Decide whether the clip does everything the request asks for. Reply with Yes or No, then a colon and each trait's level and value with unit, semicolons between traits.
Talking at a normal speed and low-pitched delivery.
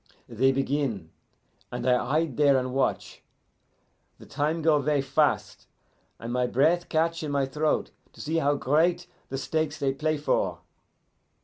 No: average, 150 wpm; medium, 145 Hz